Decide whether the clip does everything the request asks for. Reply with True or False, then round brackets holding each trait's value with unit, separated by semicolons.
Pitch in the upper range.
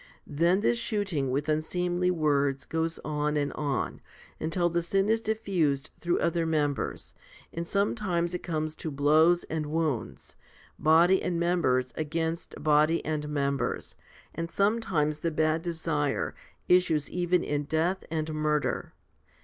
False (160 Hz)